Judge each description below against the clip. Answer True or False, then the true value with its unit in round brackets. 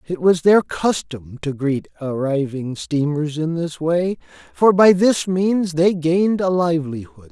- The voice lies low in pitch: False (165 Hz)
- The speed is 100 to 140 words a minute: False (155 wpm)